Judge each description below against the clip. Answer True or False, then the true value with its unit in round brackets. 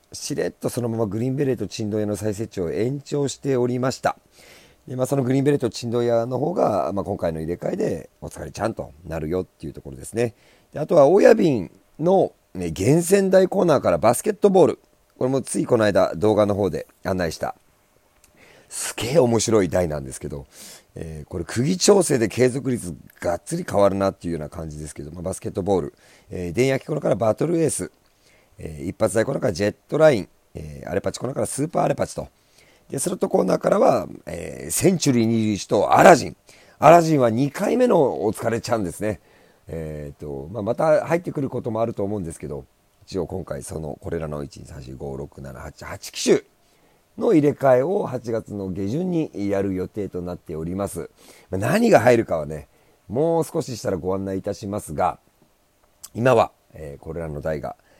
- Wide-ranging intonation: True (6.9 semitones)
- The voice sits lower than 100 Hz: False (105 Hz)